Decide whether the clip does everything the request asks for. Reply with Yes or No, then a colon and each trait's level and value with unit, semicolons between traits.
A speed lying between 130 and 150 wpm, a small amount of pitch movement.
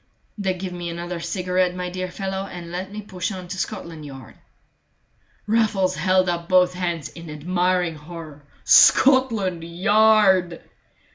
Yes: average, 140 wpm; narrow, 1.9 semitones